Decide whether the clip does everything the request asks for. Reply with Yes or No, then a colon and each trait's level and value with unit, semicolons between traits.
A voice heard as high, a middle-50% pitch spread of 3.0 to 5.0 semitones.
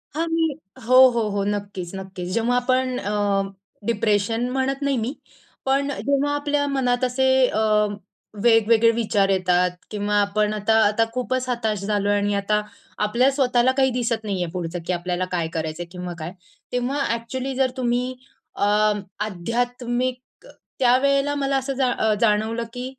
Yes: high, 230 Hz; average, 4.1 semitones